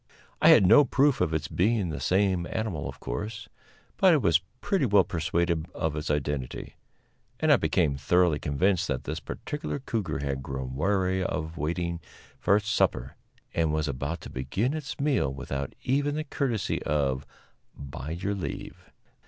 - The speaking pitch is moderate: No, very low, 85 Hz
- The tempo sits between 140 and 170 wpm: Yes, average, 165 wpm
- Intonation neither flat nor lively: No, wide, 6.4 semitones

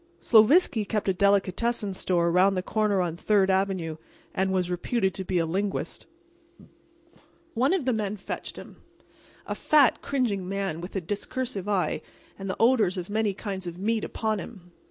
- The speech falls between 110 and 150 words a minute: No, average, 165 wpm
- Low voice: No, high, 195 Hz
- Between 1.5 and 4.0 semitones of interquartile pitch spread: Yes, average, 3.0 semitones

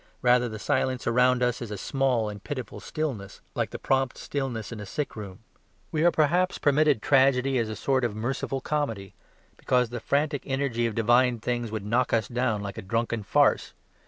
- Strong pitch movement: No, average, 3.4 semitones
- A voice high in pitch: No, low, 125 Hz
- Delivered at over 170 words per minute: Yes, average, 190 wpm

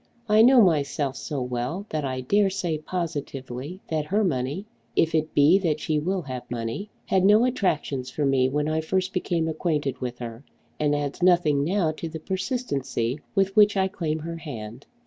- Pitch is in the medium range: Yes, medium, 155 Hz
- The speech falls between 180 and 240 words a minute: Yes, average, 185 wpm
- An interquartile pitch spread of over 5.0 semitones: Yes, wide, 5.4 semitones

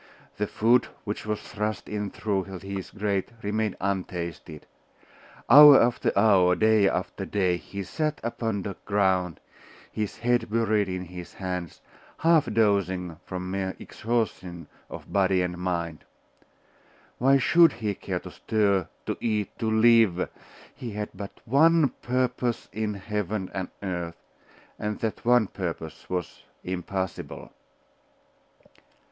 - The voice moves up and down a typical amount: Yes, average, 3.3 semitones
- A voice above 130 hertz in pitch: No, low, 100 Hz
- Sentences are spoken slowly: Yes, slow, 130 wpm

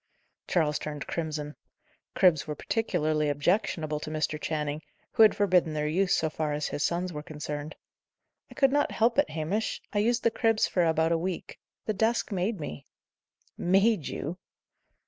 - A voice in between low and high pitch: Yes, medium, 165 Hz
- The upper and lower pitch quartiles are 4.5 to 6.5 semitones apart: Yes, average, 5.2 semitones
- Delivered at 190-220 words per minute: No, average, 165 wpm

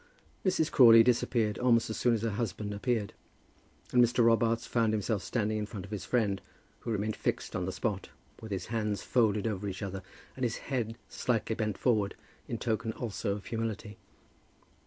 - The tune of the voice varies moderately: No, narrow, 2.2 semitones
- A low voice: Yes, low, 110 Hz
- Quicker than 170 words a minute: Yes, average, 180 wpm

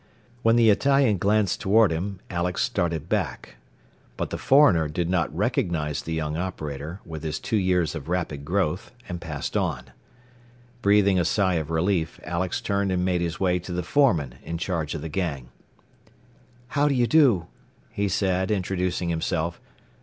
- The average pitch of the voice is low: Yes, very low, 90 Hz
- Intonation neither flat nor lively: Yes, average, 3.6 semitones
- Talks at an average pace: Yes, average, 165 wpm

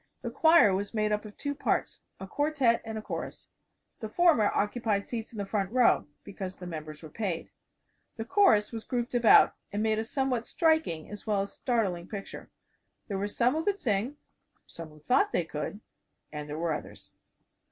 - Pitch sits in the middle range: No, high, 215 Hz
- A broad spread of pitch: No, average, 4.3 semitones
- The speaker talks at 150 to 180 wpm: No, average, 190 wpm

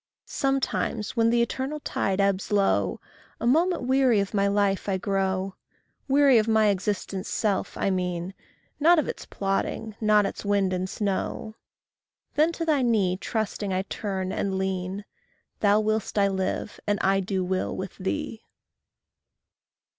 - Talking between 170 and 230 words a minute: No, average, 150 wpm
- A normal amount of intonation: Yes, average, 3.2 semitones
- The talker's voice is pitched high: Yes, high, 205 Hz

